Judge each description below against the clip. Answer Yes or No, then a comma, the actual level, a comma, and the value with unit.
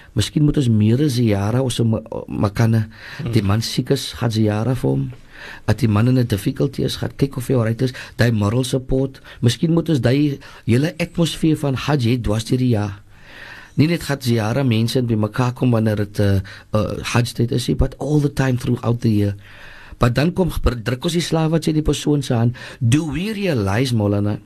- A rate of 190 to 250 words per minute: No, average, 180 wpm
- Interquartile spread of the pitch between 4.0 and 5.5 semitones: Yes, average, 4.6 semitones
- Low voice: Yes, low, 120 Hz